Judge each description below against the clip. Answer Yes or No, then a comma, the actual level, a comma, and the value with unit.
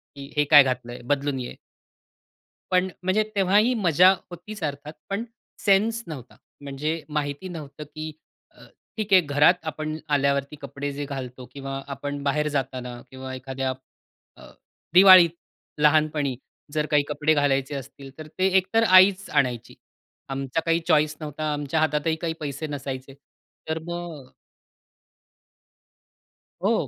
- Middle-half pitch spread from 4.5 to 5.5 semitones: No, average, 3.4 semitones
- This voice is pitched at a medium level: Yes, medium, 150 Hz